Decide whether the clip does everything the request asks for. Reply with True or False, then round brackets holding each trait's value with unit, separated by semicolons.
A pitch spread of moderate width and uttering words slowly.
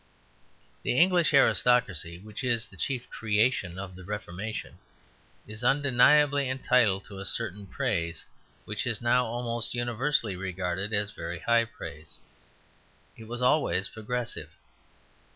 True (4.2 semitones; 125 wpm)